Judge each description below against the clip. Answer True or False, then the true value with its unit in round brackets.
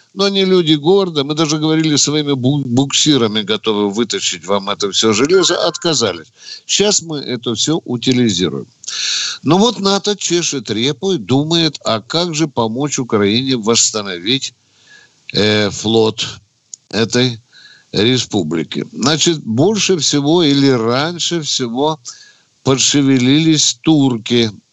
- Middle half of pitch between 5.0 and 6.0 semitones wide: True (5.6 semitones)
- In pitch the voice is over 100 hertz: True (135 Hz)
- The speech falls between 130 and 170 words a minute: False (110 wpm)